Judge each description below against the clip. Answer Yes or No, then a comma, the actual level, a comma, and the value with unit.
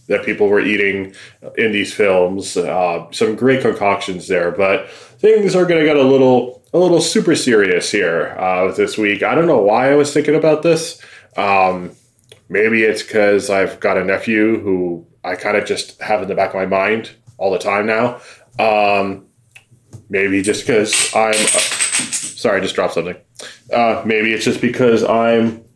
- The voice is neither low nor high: No, low, 110 Hz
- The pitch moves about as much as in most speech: No, wide, 6.3 semitones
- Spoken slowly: No, average, 180 wpm